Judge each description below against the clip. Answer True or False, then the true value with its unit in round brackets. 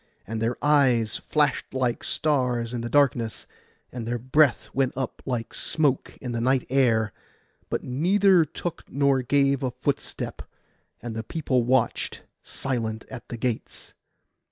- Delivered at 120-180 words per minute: True (145 wpm)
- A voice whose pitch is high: False (130 Hz)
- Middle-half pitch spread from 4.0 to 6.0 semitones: False (3.0 semitones)